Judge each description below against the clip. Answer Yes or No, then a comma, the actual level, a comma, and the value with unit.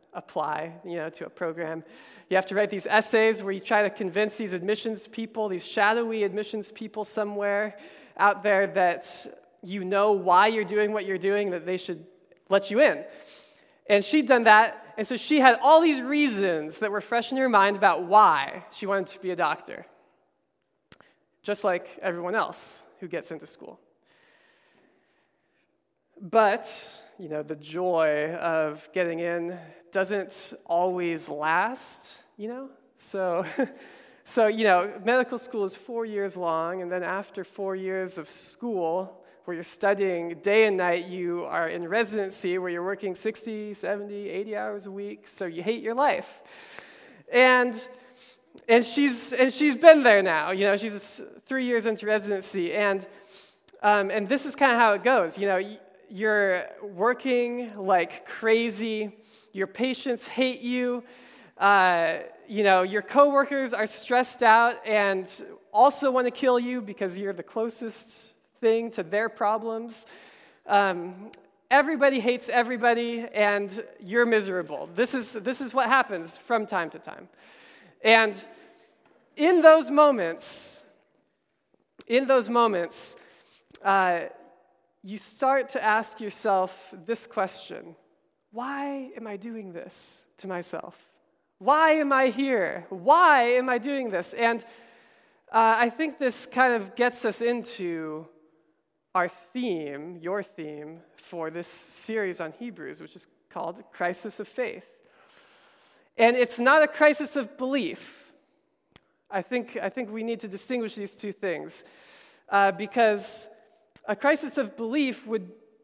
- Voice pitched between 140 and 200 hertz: No, high, 215 Hz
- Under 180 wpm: Yes, average, 150 wpm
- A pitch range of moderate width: Yes, average, 4.3 semitones